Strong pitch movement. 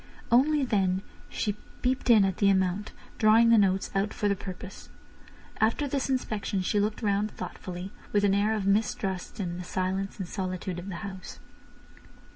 No: narrow, 2.4 semitones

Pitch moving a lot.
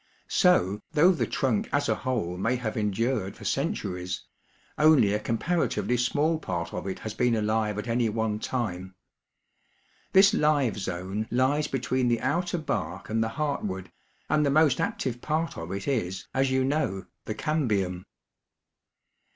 Yes: wide, 5.9 semitones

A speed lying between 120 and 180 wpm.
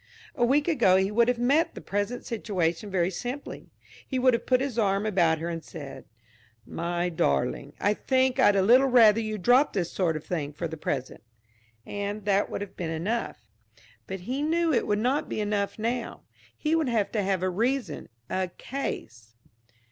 No: average, 190 wpm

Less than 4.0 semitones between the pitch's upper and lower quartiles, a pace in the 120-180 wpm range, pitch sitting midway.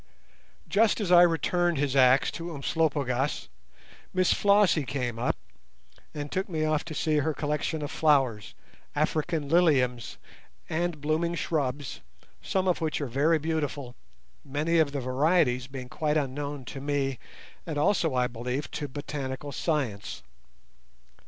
Yes: average, 3.4 semitones; average, 140 wpm; medium, 145 Hz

